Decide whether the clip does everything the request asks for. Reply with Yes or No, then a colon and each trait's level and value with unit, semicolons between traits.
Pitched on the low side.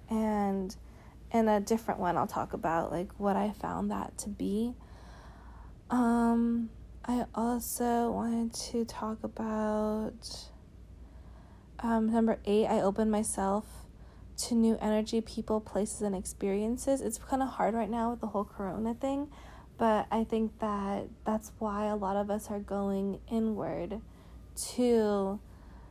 No: high, 215 Hz